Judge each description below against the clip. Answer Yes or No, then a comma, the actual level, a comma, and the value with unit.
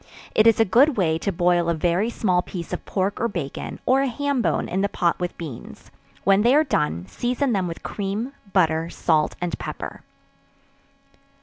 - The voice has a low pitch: No, high, 190 Hz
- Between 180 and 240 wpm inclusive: Yes, average, 190 wpm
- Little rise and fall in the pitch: No, wide, 5.5 semitones